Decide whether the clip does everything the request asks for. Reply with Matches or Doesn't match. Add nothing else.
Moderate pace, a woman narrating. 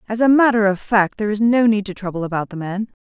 Doesn't match